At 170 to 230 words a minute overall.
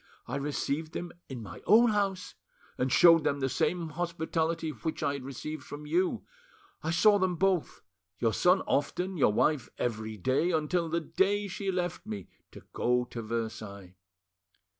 No: average, 160 wpm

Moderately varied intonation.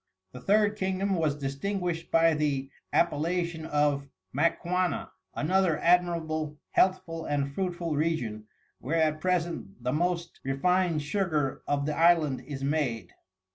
Yes: average, 3.6 semitones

